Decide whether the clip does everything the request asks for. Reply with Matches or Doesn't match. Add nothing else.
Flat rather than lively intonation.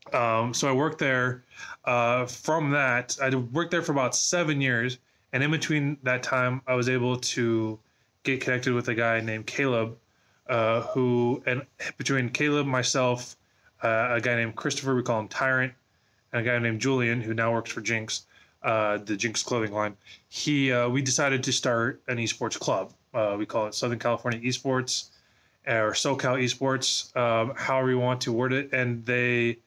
Matches